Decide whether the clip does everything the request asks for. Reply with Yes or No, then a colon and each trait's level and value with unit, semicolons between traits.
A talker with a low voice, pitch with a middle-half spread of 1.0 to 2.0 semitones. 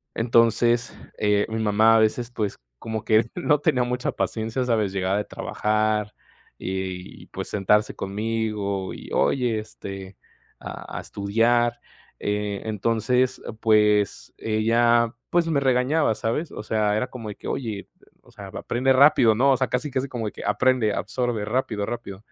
No: low, 110 Hz; average, 2.9 semitones